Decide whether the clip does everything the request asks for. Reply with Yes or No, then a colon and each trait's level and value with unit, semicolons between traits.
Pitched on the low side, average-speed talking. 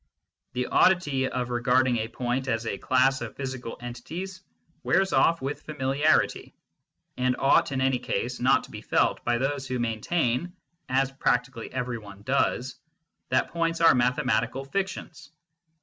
Yes: low, 130 Hz; average, 150 wpm